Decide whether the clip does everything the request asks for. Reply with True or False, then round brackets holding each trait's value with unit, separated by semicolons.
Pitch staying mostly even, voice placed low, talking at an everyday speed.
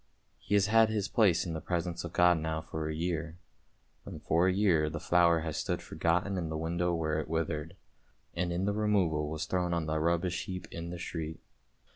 False (2.3 semitones; 85 Hz; 215 wpm)